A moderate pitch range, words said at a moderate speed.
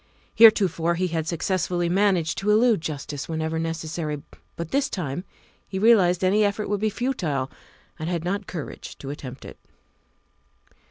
Yes: average, 4.2 semitones; average, 150 wpm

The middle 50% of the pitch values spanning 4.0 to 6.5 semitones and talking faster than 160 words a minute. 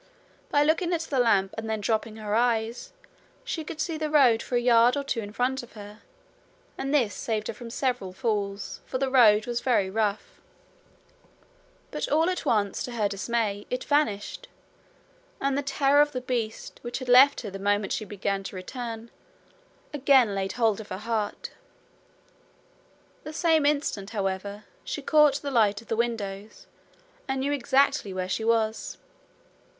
Yes: average, 4.7 semitones; average, 170 wpm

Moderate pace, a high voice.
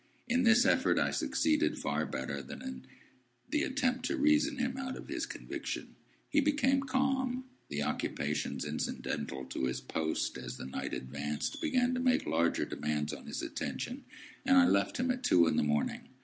Yes: average, 175 wpm; very high, 250 Hz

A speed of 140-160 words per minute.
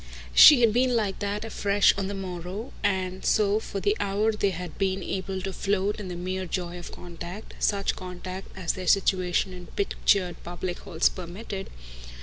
No: average, 175 wpm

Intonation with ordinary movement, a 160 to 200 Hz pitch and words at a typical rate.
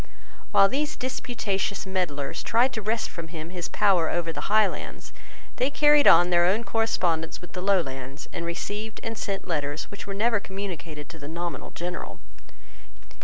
Yes: average, 4.6 semitones; medium, 185 Hz; average, 165 wpm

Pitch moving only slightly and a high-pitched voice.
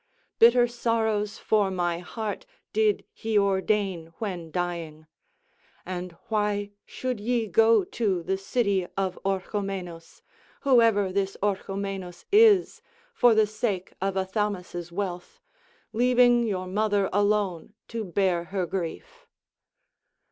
No: average, 3.1 semitones; high, 200 Hz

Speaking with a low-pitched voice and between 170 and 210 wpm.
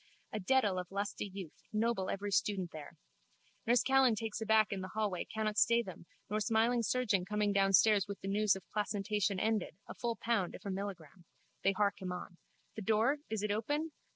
No: high, 210 Hz; average, 185 wpm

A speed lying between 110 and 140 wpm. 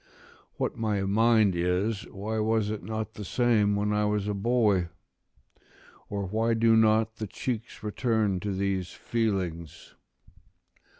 Yes: slow, 135 wpm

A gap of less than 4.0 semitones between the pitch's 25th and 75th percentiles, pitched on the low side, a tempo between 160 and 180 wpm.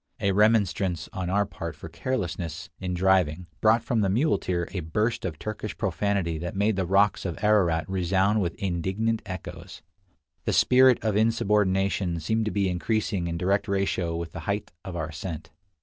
Yes: average, 3.4 semitones; very low, 95 Hz; average, 170 wpm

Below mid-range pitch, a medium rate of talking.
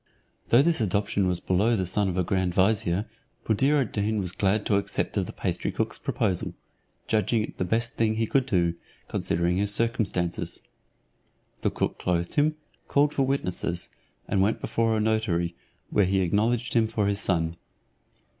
Yes: low, 100 Hz; average, 175 wpm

